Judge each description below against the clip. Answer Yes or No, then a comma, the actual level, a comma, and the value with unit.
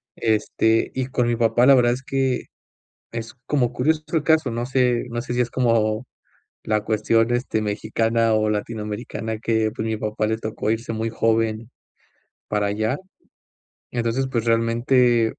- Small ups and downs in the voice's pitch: Yes, narrow, 1.9 semitones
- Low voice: Yes, low, 115 Hz